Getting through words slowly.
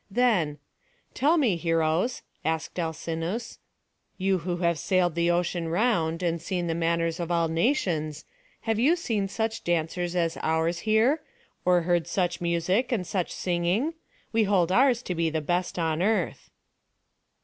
No: average, 150 wpm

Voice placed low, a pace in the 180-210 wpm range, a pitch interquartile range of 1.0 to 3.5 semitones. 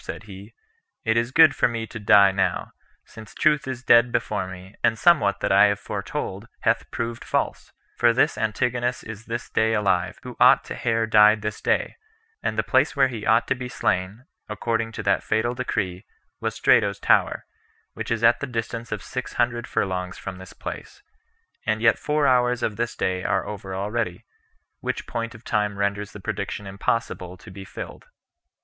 Yes: low, 110 Hz; average, 190 wpm; average, 3.0 semitones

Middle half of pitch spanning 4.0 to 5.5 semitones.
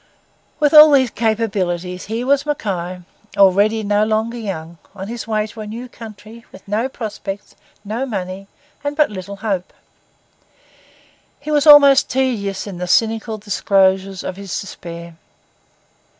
No: average, 3.5 semitones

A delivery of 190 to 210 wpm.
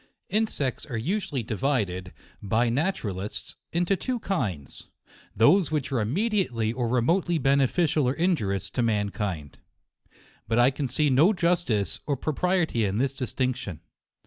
No: slow, 135 wpm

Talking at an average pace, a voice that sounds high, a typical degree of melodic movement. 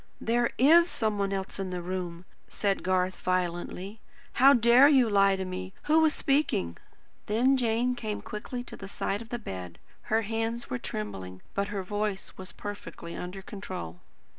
Yes: average, 170 wpm; high, 200 Hz; average, 4.4 semitones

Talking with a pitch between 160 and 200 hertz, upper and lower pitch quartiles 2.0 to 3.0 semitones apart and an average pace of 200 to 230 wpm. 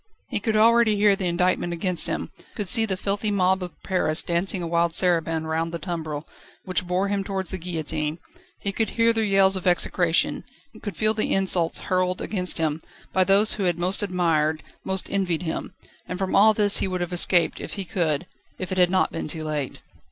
Yes: medium, 185 Hz; average, 2.7 semitones; fast, 205 wpm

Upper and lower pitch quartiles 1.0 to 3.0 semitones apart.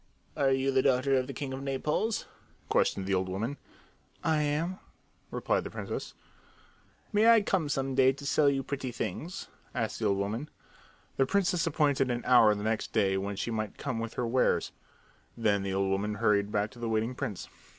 No: average, 5.0 semitones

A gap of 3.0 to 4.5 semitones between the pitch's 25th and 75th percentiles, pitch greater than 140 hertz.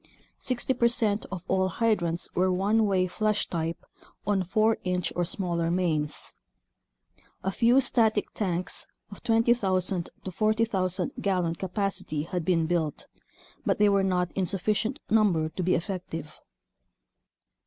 Yes: average, 3.5 semitones; high, 190 Hz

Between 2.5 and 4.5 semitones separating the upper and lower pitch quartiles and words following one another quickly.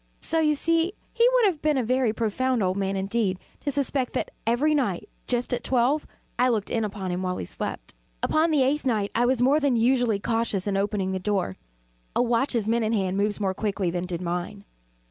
No: average, 5.2 semitones; fast, 210 wpm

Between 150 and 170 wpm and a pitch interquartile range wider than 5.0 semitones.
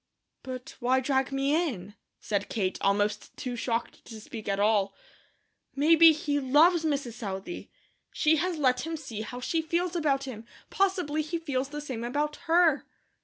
Yes: average, 165 wpm; wide, 5.4 semitones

